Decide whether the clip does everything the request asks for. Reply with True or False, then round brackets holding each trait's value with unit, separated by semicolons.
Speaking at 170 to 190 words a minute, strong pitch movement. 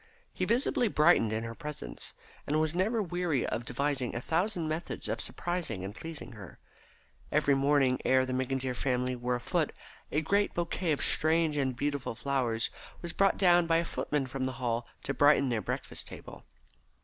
False (175 wpm; 4.8 semitones)